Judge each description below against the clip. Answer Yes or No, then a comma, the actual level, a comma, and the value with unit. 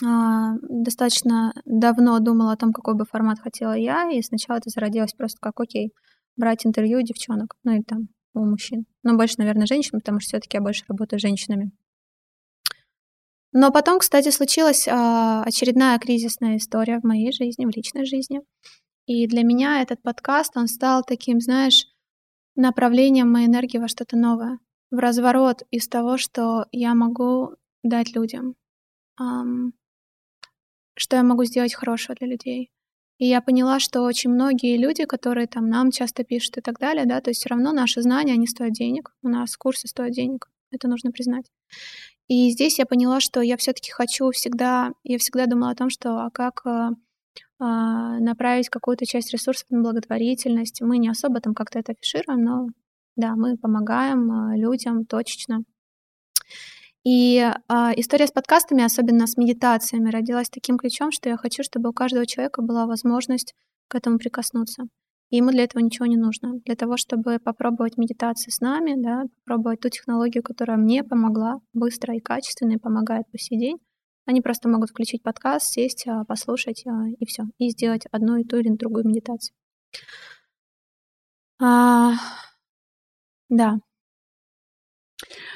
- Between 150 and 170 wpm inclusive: Yes, average, 155 wpm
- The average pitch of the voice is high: Yes, high, 240 Hz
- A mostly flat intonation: Yes, narrow, 1.6 semitones